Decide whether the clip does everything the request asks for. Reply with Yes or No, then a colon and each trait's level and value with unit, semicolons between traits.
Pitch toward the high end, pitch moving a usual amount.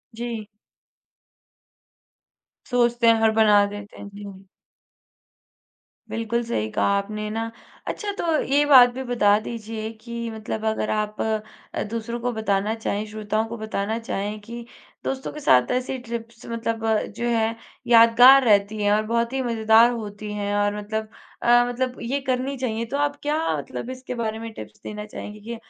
No: high, 225 Hz; narrow, 2.2 semitones